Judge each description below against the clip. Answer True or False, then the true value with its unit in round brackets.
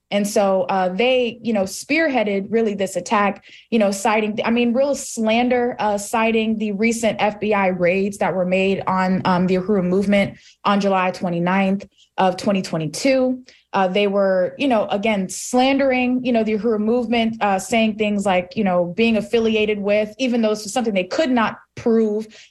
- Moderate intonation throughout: True (3.0 semitones)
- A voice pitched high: True (210 Hz)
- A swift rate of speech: False (175 wpm)